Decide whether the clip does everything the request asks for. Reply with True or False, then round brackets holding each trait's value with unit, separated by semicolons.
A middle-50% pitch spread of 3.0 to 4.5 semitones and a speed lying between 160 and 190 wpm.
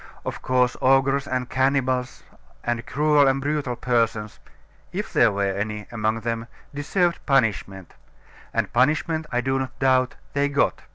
False (3.3 semitones; 145 wpm)